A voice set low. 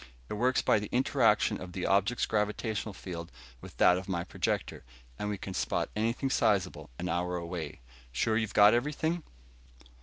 Yes: low, 105 Hz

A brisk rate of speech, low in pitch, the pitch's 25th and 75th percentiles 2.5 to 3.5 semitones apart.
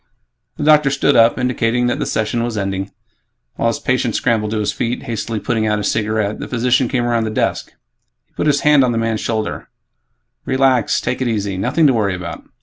Yes: fast, 210 wpm; low, 115 Hz; average, 2.8 semitones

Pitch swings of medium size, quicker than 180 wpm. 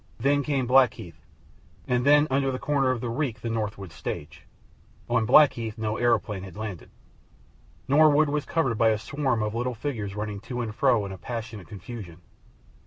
No: average, 4.0 semitones; average, 175 wpm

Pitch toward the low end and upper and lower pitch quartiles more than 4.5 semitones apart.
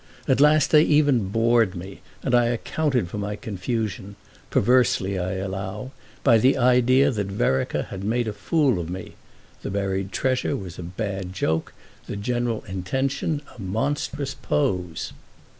Yes: low, 105 Hz; average, 5.1 semitones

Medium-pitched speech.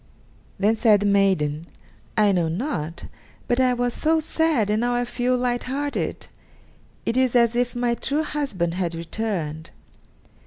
No: high, 235 Hz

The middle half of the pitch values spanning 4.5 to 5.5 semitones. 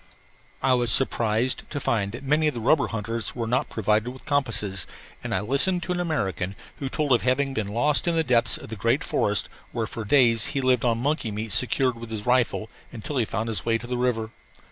No: average, 3.5 semitones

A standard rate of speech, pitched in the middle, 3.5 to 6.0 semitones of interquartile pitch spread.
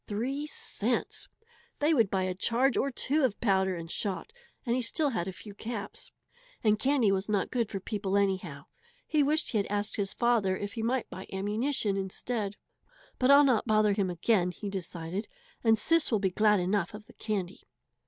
No: average, 195 wpm; high, 210 Hz; average, 4.0 semitones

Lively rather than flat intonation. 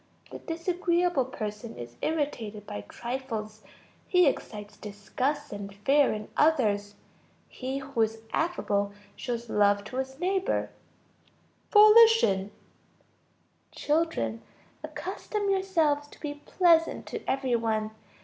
Yes: wide, 7.6 semitones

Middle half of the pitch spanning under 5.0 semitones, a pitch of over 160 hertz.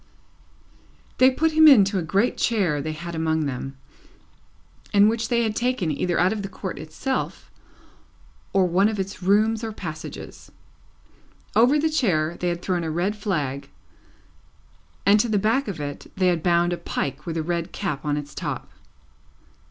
No: average, 5.3 semitones; medium, 185 Hz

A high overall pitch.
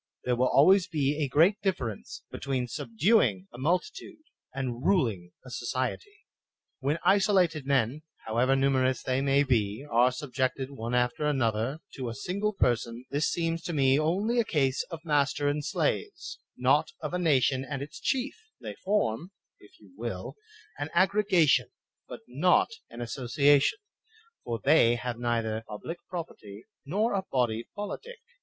No: medium, 140 Hz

